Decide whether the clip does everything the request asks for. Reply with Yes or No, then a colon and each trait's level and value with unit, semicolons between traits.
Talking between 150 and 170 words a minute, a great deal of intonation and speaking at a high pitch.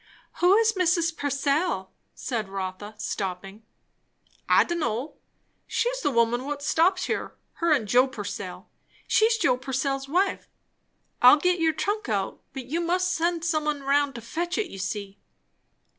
Yes: average, 155 wpm; wide, 6.8 semitones; very high, 285 Hz